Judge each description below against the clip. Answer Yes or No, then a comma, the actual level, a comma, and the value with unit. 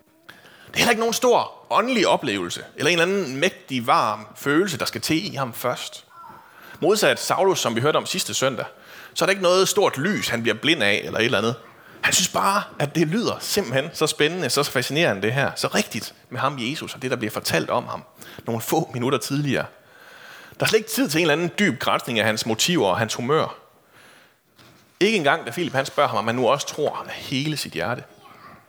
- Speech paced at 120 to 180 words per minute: No, average, 220 wpm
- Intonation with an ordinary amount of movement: No, wide, 7.5 semitones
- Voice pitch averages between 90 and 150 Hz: No, medium, 160 Hz